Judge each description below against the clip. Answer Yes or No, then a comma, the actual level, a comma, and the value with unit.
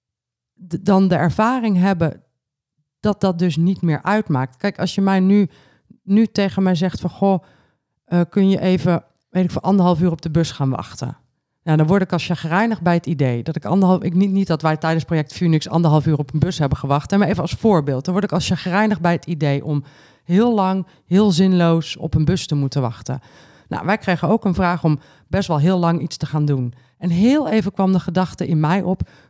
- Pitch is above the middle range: No, medium, 175 Hz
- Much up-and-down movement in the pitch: No, average, 3.6 semitones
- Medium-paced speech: No, fast, 225 wpm